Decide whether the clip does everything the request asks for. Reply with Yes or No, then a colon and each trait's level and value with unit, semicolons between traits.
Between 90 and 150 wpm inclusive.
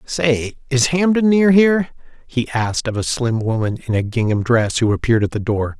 No: fast, 205 wpm